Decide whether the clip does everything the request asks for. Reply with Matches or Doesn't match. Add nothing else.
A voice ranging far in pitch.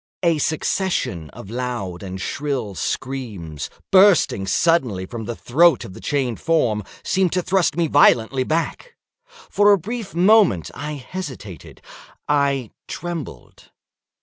Matches